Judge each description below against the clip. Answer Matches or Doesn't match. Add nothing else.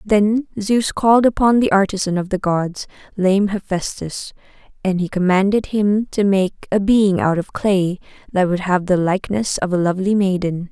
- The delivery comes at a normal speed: Matches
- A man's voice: Doesn't match